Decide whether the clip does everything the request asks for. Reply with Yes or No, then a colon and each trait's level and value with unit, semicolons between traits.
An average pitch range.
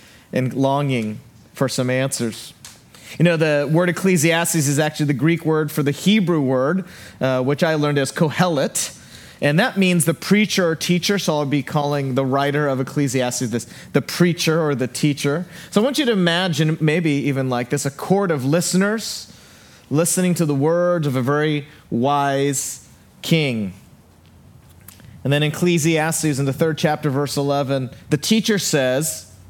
Yes: average, 3.8 semitones